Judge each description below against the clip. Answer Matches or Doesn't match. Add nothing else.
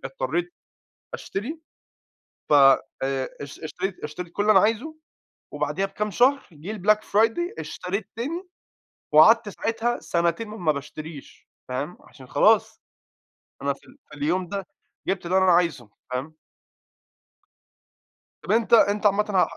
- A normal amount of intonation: Doesn't match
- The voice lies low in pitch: Doesn't match